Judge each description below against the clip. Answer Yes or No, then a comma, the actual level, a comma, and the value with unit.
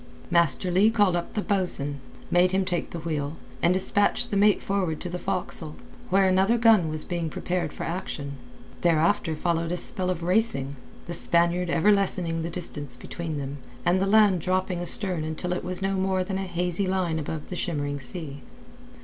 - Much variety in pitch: No, average, 2.8 semitones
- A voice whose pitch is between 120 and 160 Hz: No, medium, 175 Hz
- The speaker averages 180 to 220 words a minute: Yes, average, 185 wpm